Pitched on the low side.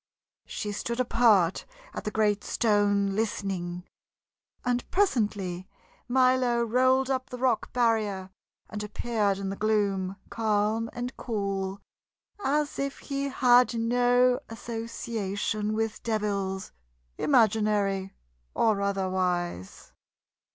No: high, 215 Hz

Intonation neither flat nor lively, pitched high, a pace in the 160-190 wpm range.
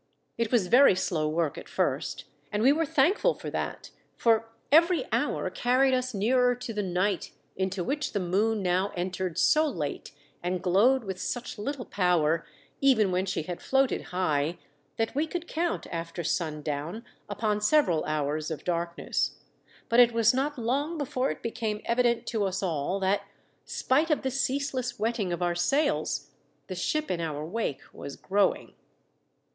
No: wide, 6.5 semitones; high, 210 Hz; average, 165 wpm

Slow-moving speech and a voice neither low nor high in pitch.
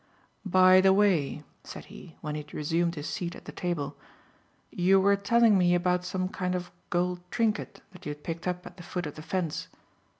No: fast, 205 wpm; medium, 180 Hz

